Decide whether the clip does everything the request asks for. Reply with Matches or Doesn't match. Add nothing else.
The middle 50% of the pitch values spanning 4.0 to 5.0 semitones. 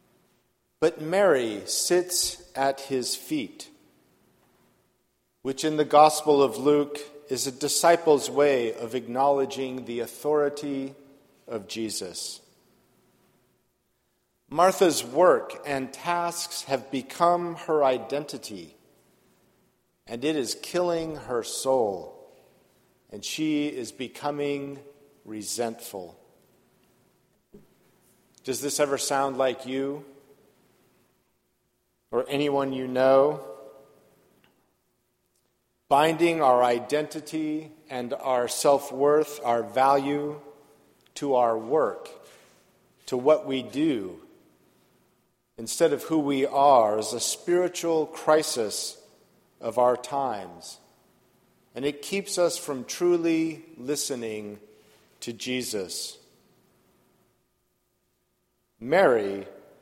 Doesn't match